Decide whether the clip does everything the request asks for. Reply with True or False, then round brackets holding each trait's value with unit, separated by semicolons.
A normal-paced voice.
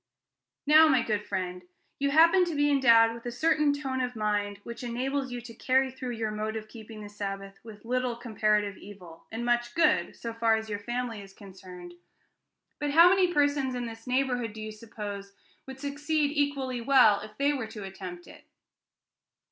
True (190 wpm)